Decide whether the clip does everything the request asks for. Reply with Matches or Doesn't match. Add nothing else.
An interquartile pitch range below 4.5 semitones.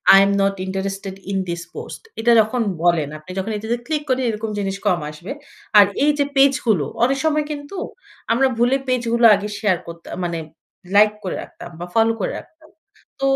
Doesn't match